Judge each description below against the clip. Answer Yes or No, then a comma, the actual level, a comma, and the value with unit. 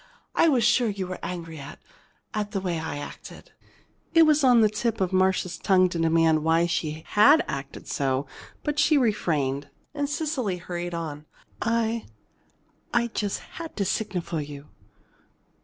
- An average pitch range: No, wide, 6.3 semitones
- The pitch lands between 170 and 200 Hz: Yes, medium, 185 Hz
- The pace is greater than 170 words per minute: No, average, 160 wpm